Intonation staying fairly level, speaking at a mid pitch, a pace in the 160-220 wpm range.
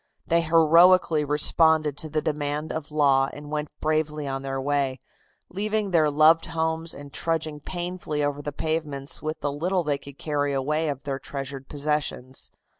Yes: narrow, 2.1 semitones; medium, 150 Hz; average, 165 wpm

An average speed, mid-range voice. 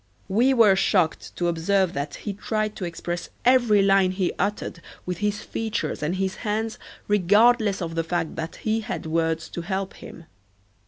No: average, 170 wpm; high, 195 Hz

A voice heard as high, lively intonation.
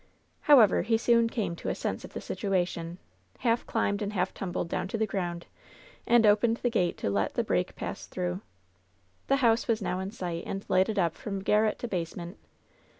No: high, 200 Hz; average, 4.3 semitones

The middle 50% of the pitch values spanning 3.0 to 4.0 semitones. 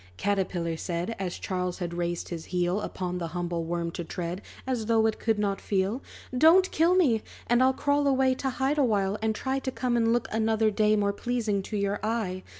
No: average, 5.3 semitones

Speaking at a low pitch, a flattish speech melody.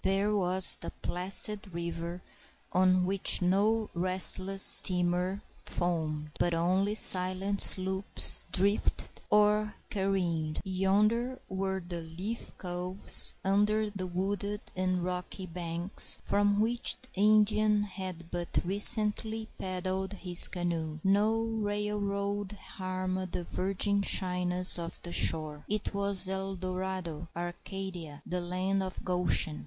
No: high, 190 Hz; narrow, 2.2 semitones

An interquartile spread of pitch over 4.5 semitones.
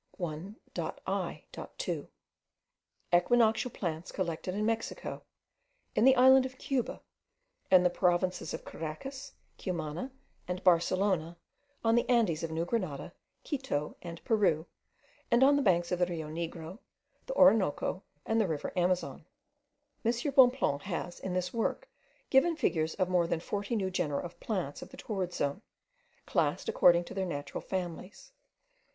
Yes: average, 5.2 semitones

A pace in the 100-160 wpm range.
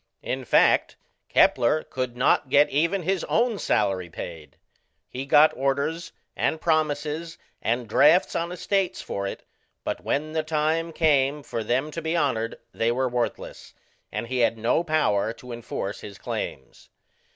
Yes: average, 150 wpm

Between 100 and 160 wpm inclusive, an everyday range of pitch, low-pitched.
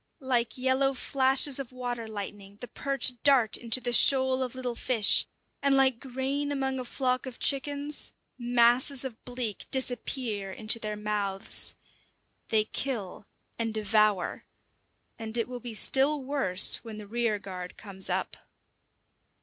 No: average, 140 wpm; average, 3.5 semitones; high, 245 Hz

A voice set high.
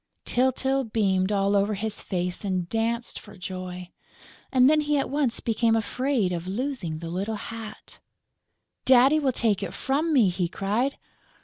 Yes: high, 220 Hz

